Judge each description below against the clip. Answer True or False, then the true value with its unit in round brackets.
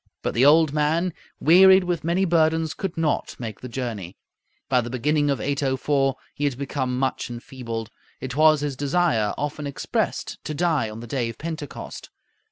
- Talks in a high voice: False (145 Hz)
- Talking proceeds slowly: False (175 wpm)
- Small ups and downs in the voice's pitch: False (4.0 semitones)